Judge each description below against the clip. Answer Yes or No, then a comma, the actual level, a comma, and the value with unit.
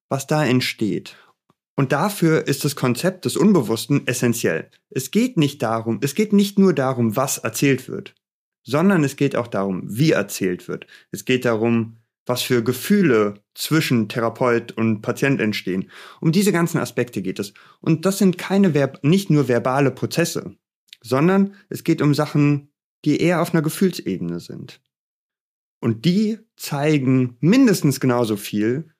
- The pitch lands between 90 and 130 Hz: No, medium, 140 Hz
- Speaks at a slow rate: No, average, 150 wpm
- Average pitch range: No, wide, 5.9 semitones